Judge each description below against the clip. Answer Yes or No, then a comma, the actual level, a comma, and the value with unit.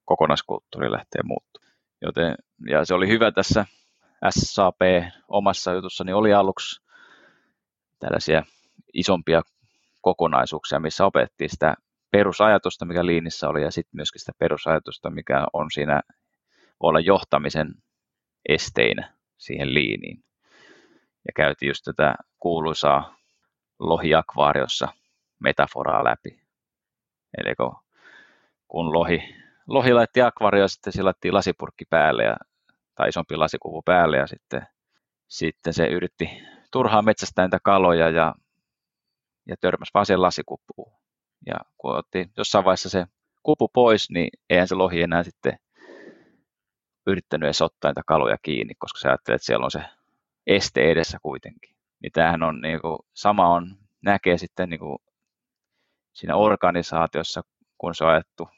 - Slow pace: Yes, slow, 125 wpm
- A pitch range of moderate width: Yes, average, 3.0 semitones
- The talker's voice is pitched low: Yes, very low, 90 Hz